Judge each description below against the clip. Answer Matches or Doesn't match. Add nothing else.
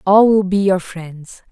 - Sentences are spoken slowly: Doesn't match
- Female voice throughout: Matches